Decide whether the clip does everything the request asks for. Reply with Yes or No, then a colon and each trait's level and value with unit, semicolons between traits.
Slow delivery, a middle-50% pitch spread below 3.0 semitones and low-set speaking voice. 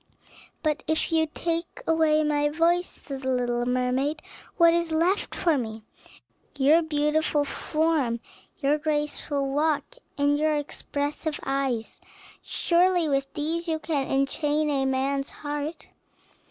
No: slow, 125 wpm; narrow, 2.6 semitones; very high, 295 Hz